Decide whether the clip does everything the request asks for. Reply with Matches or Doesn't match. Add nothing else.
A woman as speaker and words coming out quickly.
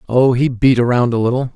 Doesn't match